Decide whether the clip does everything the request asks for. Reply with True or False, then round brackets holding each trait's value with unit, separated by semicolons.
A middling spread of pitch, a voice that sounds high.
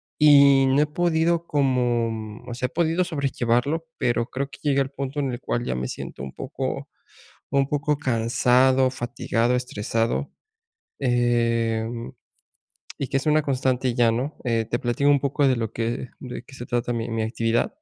False (3.1 semitones; 125 Hz)